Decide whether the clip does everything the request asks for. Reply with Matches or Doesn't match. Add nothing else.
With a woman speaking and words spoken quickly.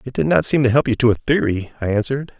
Doesn't match